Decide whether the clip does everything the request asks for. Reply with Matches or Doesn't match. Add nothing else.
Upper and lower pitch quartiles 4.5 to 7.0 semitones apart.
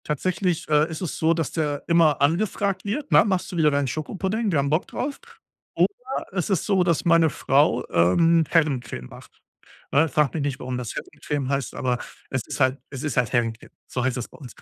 Matches